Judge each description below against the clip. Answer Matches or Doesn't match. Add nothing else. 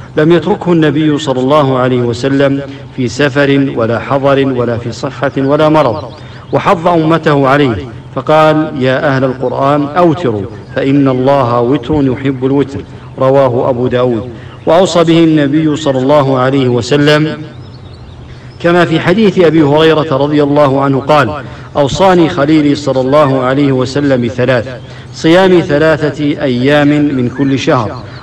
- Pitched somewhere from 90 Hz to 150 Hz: Matches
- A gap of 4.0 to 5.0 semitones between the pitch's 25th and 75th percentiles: Doesn't match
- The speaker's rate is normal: Doesn't match